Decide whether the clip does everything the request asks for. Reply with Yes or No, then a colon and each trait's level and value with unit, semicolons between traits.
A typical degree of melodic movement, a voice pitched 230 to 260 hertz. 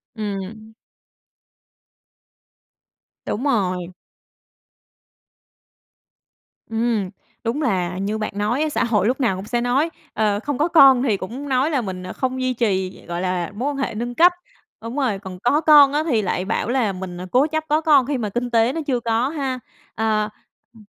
Yes: average, 4.9 semitones; high, 235 Hz